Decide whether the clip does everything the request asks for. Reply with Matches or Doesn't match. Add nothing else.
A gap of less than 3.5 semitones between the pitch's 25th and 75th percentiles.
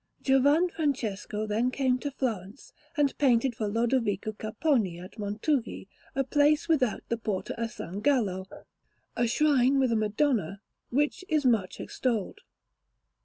Doesn't match